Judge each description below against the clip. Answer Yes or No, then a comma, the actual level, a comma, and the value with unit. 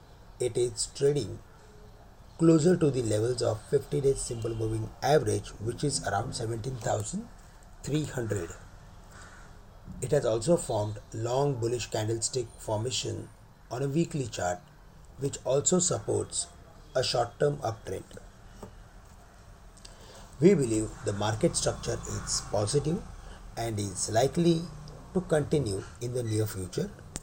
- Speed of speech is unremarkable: No, slow, 115 wpm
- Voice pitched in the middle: No, low, 115 Hz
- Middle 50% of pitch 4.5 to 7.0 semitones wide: Yes, wide, 5.6 semitones